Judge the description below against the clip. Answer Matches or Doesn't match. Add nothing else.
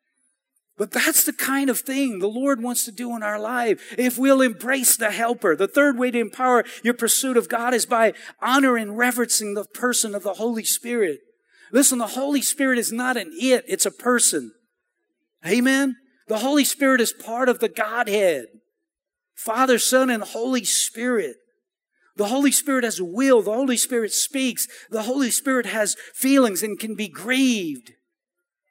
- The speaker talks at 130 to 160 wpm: Doesn't match